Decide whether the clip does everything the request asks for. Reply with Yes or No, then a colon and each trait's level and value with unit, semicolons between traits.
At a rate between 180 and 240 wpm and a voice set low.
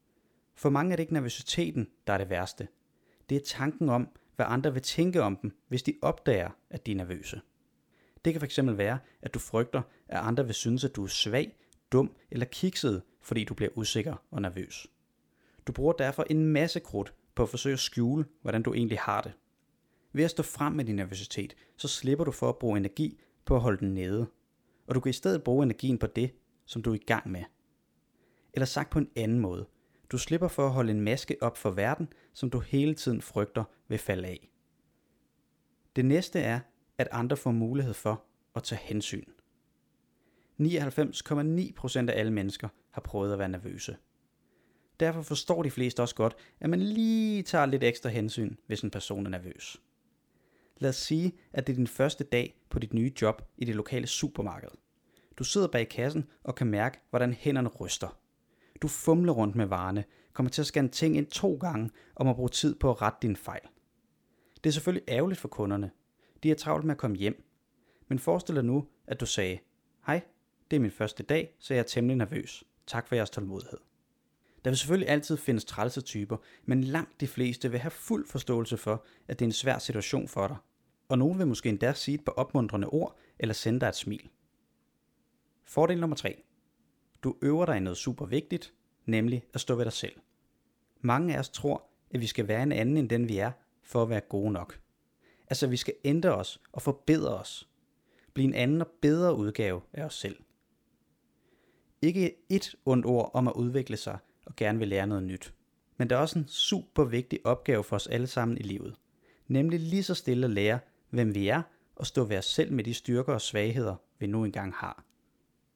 Yes: average, 200 wpm; low, 125 Hz